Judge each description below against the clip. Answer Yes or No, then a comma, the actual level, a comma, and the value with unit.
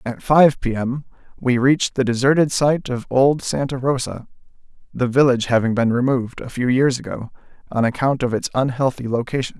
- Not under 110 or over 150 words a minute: No, average, 175 wpm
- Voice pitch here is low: Yes, low, 130 Hz